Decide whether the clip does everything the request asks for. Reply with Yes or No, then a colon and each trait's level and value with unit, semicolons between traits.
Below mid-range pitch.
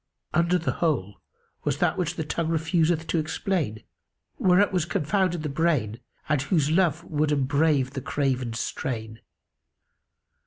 No: medium, 155 Hz